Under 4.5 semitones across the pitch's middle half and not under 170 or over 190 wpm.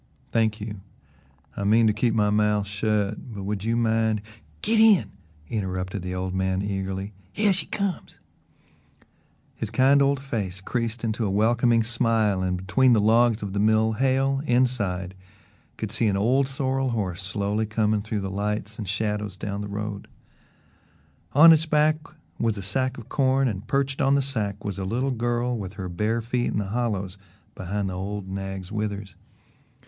Yes: average, 3.4 semitones; average, 175 wpm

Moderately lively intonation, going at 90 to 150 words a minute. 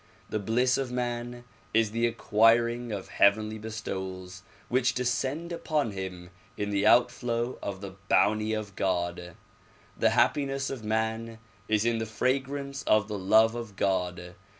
Yes: average, 3.4 semitones; average, 145 wpm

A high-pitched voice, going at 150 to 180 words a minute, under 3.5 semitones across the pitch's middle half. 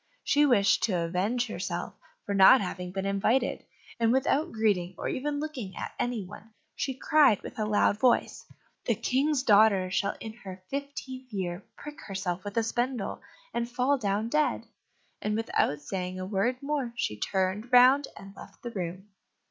No: high, 220 Hz; average, 170 wpm; average, 5.0 semitones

